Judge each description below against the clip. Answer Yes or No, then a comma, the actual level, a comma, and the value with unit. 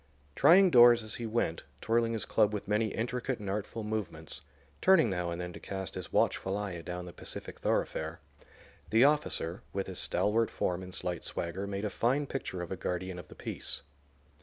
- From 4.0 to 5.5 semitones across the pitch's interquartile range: Yes, average, 4.4 semitones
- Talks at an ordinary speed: Yes, average, 190 wpm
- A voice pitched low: Yes, low, 105 Hz